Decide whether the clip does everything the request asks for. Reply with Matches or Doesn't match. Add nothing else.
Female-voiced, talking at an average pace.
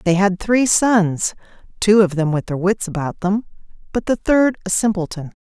Matches